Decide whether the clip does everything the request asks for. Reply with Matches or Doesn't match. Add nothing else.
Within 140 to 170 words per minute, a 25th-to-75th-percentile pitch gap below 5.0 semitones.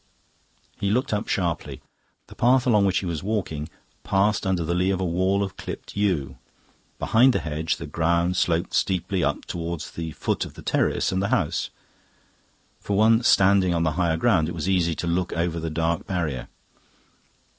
Doesn't match